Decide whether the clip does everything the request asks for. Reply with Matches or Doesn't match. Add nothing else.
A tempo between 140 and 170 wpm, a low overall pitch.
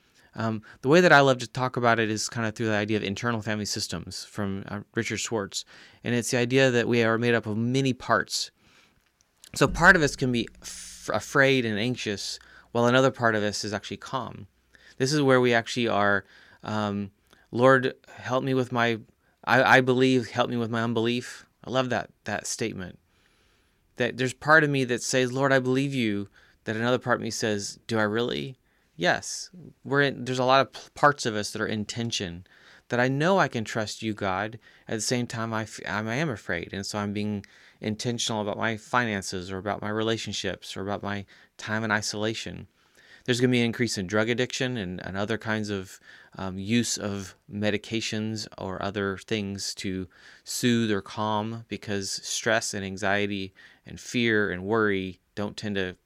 Doesn't match